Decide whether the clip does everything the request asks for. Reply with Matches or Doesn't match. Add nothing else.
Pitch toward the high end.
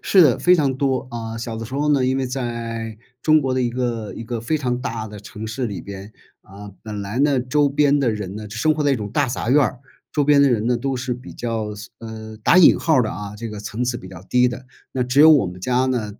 Doesn't match